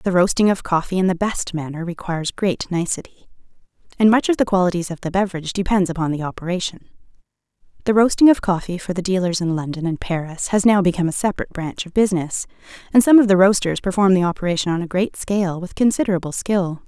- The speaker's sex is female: Yes, female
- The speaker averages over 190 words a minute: Yes, fast, 205 wpm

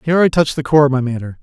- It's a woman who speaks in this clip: No, male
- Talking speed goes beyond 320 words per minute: Yes, fast, 335 wpm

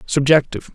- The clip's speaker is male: Yes, male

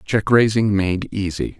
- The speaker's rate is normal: Yes, average, 150 wpm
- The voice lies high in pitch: No, low, 105 Hz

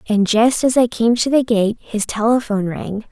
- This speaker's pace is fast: Yes, fast, 210 wpm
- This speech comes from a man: No, female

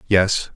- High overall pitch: No, very low, 95 Hz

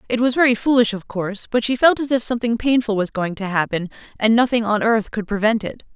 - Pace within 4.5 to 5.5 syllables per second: No, 6.1 syllables/s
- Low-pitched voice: No, high, 225 Hz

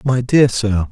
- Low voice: Yes, low, 115 Hz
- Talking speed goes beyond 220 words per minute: No, average, 200 wpm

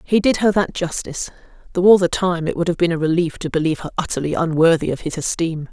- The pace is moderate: No, fast, 240 wpm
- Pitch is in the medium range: Yes, medium, 170 Hz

